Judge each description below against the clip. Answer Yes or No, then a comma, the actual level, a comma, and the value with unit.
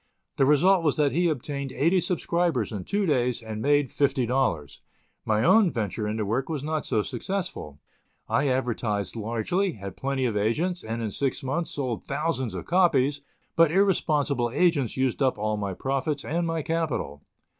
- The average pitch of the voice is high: No, low, 135 Hz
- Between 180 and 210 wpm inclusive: No, average, 170 wpm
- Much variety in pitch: Yes, wide, 6.3 semitones